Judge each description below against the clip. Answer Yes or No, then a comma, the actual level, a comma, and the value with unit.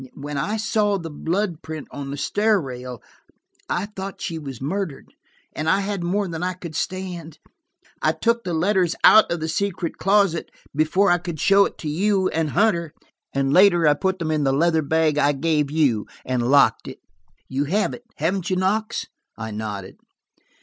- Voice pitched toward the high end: No, medium, 165 Hz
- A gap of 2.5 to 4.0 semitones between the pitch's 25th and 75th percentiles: No, average, 4.9 semitones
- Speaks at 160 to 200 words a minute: Yes, average, 185 wpm